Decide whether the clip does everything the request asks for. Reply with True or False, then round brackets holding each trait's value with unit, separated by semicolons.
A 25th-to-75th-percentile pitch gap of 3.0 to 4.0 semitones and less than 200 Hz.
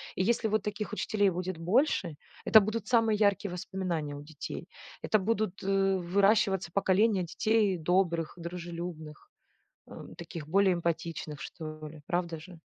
True (3.3 semitones; 185 Hz)